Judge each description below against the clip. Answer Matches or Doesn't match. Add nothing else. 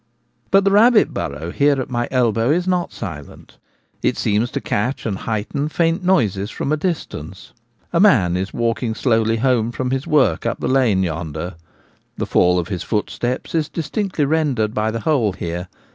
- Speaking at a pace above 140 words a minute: Matches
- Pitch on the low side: Matches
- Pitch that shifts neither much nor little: Doesn't match